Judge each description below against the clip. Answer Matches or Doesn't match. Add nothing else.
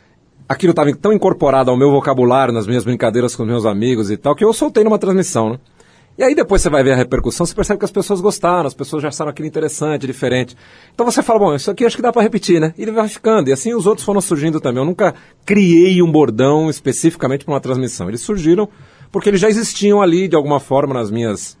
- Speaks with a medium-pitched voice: Matches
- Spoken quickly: Matches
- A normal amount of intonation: Doesn't match